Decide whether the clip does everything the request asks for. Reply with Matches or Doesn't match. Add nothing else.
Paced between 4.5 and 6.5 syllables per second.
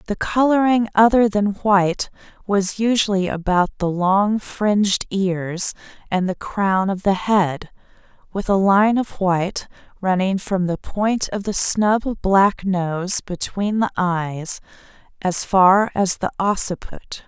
Doesn't match